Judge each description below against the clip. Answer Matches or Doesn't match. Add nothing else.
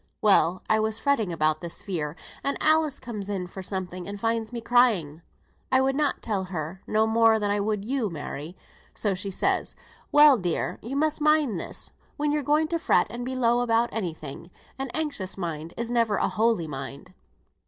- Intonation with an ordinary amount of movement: Doesn't match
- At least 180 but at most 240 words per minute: Matches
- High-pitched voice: Matches